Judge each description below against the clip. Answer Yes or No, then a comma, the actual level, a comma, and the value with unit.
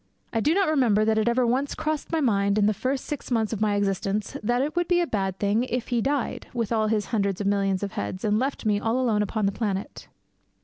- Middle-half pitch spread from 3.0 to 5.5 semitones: Yes, average, 4.1 semitones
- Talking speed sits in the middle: No, fast, 255 wpm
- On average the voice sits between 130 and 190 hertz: No, high, 220 Hz